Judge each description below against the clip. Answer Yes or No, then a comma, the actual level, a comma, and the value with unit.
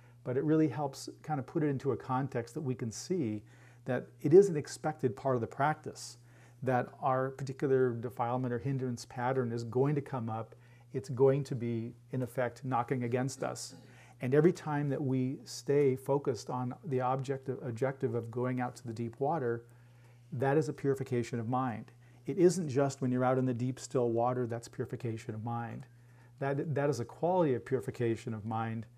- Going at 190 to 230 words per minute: Yes, average, 195 wpm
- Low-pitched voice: Yes, low, 125 Hz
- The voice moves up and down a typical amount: No, narrow, 2.3 semitones